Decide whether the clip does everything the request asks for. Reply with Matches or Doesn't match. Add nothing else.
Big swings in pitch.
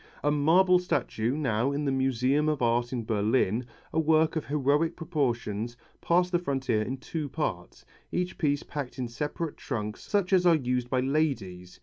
Doesn't match